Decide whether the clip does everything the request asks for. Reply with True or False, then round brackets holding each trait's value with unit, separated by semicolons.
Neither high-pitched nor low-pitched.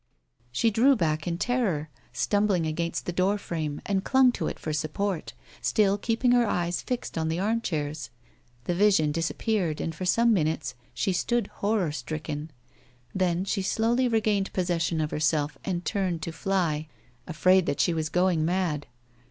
True (180 Hz)